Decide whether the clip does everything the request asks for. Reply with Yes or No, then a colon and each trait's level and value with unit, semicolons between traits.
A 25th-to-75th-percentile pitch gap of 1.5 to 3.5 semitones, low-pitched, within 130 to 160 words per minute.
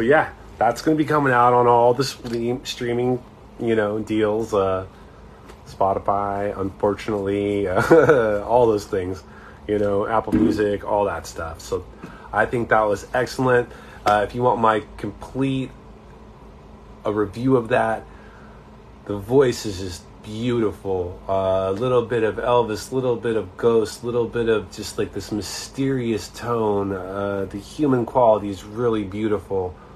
Yes: average, 3.2 semitones; low, 110 Hz; average, 155 wpm